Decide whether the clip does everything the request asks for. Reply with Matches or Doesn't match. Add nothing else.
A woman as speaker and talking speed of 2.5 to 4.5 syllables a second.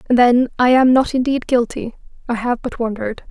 Doesn't match